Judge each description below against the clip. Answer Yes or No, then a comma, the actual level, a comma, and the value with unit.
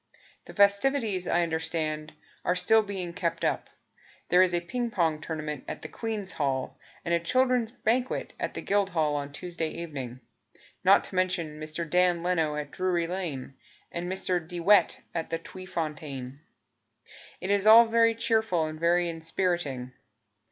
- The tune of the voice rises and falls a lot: No, average, 3.9 semitones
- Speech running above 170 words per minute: No, average, 155 wpm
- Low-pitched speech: No, medium, 175 Hz